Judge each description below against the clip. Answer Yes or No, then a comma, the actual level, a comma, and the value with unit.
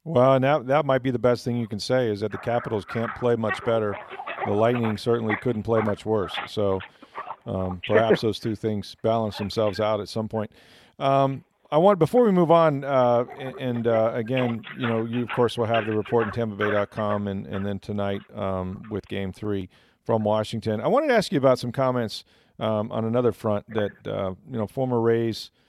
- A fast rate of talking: Yes, fast, 210 wpm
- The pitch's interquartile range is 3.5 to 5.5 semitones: No, average, 3.0 semitones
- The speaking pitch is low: Yes, low, 115 Hz